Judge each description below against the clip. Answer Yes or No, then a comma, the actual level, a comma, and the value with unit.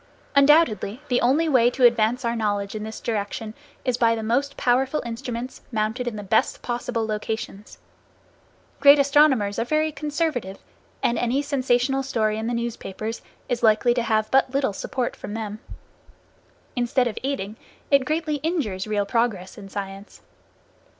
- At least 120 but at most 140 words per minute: No, average, 155 wpm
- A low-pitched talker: No, high, 235 Hz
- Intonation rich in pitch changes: No, average, 3.8 semitones